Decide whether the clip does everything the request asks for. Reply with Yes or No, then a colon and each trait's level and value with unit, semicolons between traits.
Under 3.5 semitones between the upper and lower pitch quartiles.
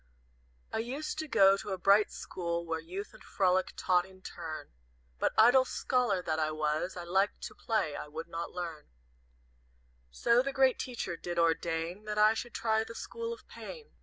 No: wide, 5.4 semitones